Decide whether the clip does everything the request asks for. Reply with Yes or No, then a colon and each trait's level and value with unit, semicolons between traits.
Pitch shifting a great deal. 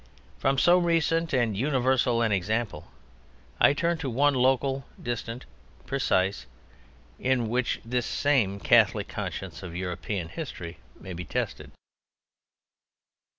Yes: wide, 5.8 semitones